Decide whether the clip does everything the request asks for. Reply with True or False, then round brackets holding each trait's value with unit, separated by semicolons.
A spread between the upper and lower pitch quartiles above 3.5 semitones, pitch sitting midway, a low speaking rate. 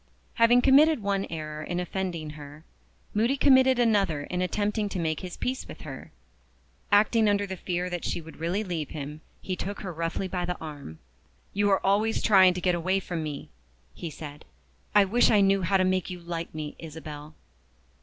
False (4.0 semitones; 180 Hz; 190 wpm)